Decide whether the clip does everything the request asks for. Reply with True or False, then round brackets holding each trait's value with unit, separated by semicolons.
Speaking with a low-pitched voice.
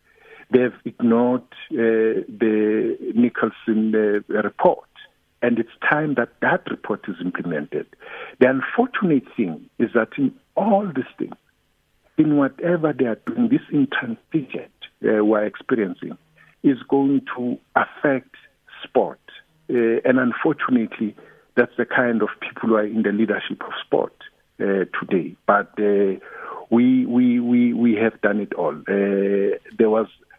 True (120 Hz)